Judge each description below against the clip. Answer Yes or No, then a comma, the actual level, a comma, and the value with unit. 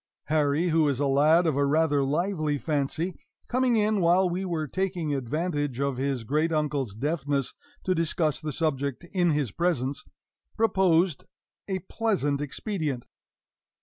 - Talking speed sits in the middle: Yes, average, 145 wpm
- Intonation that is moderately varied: Yes, average, 3.9 semitones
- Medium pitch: Yes, medium, 155 Hz